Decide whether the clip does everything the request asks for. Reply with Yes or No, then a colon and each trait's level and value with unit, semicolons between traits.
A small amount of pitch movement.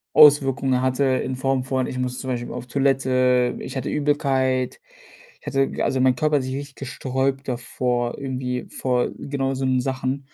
Yes: narrow, 1.2 semitones